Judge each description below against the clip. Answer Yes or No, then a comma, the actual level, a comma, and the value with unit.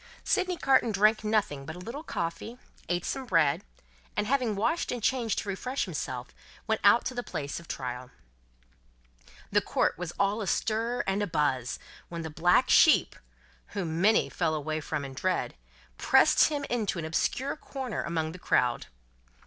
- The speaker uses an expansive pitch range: Yes, wide, 7.0 semitones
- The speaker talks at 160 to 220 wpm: Yes, average, 165 wpm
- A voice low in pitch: No, high, 195 Hz